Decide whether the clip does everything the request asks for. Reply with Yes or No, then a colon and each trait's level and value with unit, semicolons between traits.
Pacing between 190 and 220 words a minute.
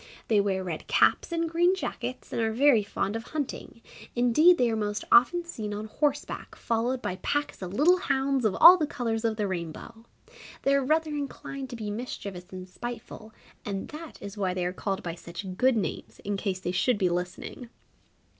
Yes: average, 195 wpm